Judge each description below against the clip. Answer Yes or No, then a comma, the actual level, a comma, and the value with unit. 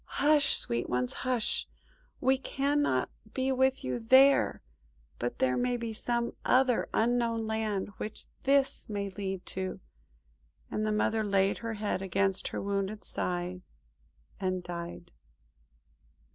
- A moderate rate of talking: No, slow, 130 wpm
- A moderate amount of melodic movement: Yes, average, 4.9 semitones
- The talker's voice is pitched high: Yes, high, 215 Hz